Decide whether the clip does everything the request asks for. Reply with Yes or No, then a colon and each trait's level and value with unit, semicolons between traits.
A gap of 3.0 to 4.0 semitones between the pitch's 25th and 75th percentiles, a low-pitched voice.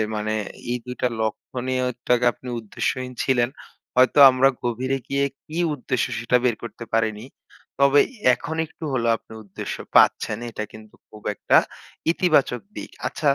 No: narrow, 2.6 semitones; low, 125 Hz